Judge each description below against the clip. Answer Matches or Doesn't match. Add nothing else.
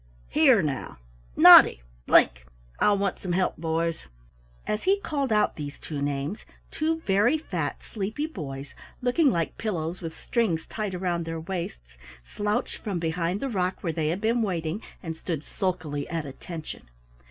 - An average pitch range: Matches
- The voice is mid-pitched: Matches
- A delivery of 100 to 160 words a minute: Matches